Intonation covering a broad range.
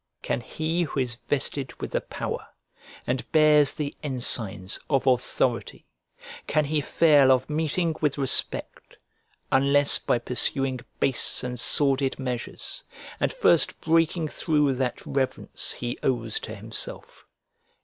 No: average, 3.3 semitones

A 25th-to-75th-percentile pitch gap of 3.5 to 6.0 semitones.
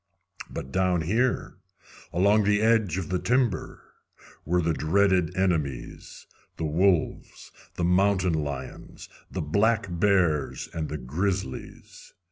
Yes: average, 4.3 semitones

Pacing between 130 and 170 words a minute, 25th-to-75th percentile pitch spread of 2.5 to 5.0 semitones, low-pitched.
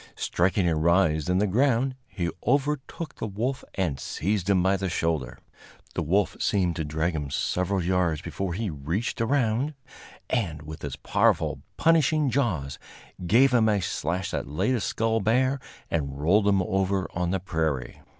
No: average, 165 wpm; wide, 5.6 semitones; very low, 95 Hz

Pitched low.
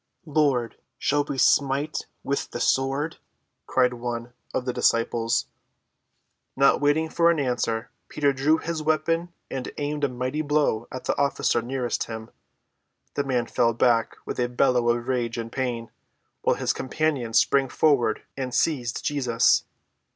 Yes: low, 130 Hz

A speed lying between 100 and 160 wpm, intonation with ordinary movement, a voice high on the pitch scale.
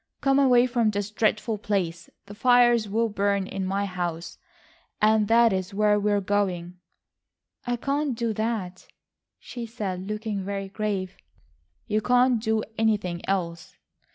Yes: average, 145 wpm; average, 3.0 semitones; high, 210 Hz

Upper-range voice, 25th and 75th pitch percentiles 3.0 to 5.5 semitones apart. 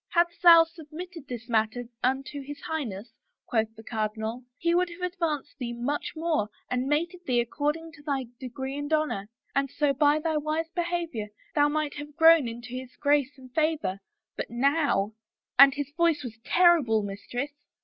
Yes: very high, 290 Hz; average, 4.8 semitones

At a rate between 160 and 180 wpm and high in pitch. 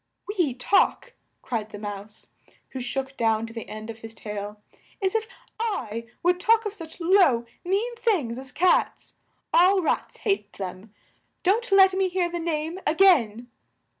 Yes: average, 165 wpm; very high, 315 Hz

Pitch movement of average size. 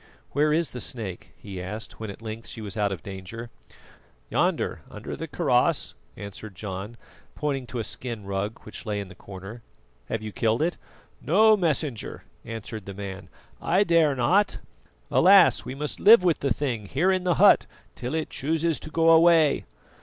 No: wide, 7.8 semitones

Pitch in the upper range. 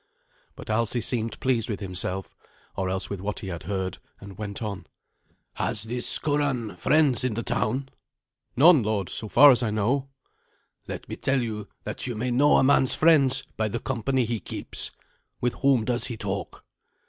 No: low, 115 Hz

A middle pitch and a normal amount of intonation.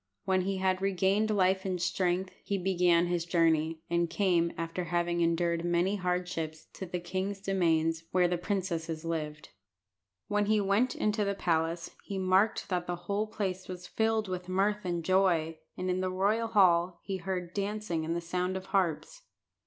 No: medium, 180 Hz; narrow, 2.3 semitones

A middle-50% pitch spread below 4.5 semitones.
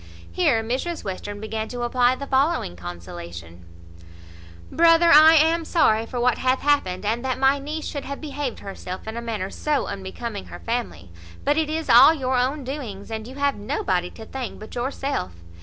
No: wide, 5.6 semitones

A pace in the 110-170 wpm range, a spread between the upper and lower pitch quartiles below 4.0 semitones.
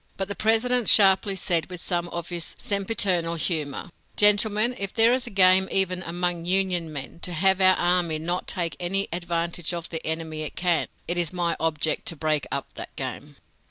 No: average, 190 wpm; narrow, 2.6 semitones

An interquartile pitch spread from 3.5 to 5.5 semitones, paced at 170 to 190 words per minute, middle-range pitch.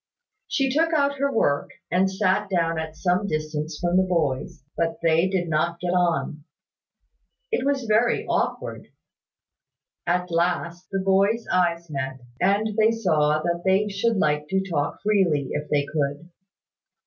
No: average, 4.2 semitones; average, 150 wpm; medium, 175 Hz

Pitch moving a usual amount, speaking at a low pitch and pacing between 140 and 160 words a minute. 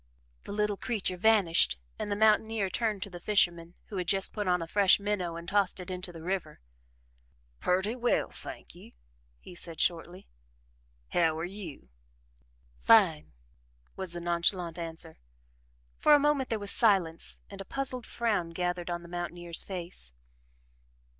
No: average, 3.4 semitones; medium, 185 Hz; average, 155 wpm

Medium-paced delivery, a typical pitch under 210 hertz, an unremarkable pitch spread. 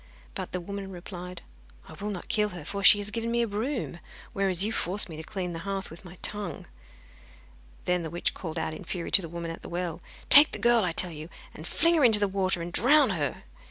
No: fast, 240 wpm; high, 190 Hz; average, 3.4 semitones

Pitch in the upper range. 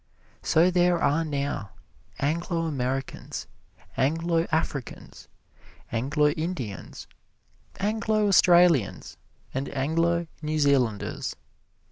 No: medium, 155 Hz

